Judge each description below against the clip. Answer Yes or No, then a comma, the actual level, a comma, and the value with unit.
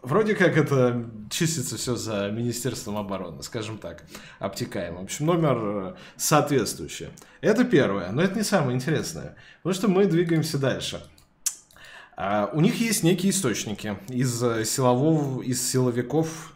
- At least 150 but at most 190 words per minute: No, average, 130 wpm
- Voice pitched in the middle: No, low, 130 Hz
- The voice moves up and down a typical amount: No, wide, 6.5 semitones